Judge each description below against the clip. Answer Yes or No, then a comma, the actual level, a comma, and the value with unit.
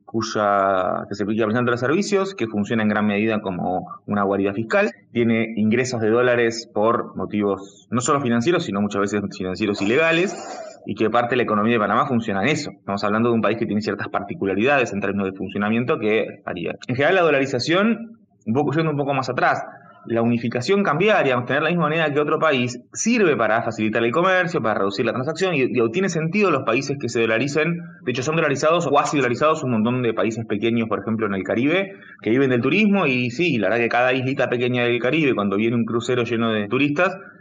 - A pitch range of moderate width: No, wide, 6.2 semitones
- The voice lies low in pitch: Yes, low, 120 Hz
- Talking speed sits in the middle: No, fast, 210 wpm